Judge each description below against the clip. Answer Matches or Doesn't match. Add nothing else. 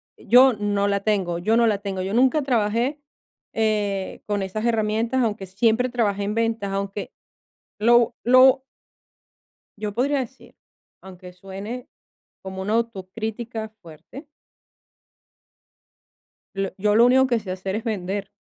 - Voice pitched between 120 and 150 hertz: Doesn't match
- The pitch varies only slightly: Doesn't match